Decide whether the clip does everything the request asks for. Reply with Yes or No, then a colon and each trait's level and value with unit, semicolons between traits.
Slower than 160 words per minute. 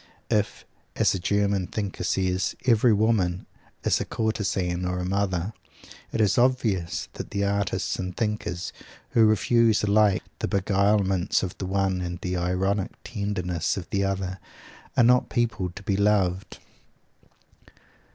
Yes: average, 140 wpm